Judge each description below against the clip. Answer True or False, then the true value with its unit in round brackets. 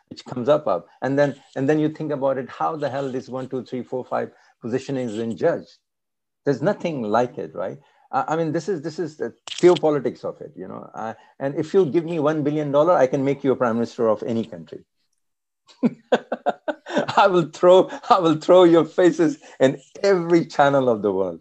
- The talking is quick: True (215 wpm)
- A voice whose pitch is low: False (145 Hz)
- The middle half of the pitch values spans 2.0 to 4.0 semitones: False (4.9 semitones)